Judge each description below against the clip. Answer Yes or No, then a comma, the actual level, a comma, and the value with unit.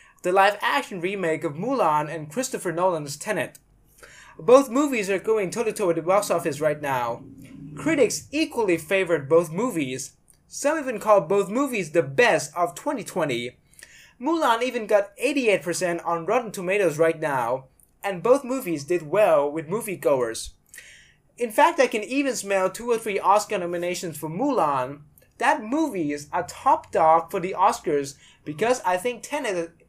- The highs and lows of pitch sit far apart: Yes, wide, 6.6 semitones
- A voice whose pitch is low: No, high, 195 Hz